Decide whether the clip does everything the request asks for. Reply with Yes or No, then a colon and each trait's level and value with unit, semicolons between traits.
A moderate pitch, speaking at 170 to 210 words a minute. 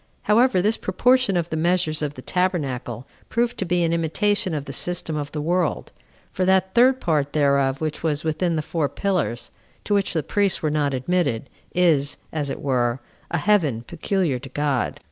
Yes: medium, 160 Hz; average, 185 wpm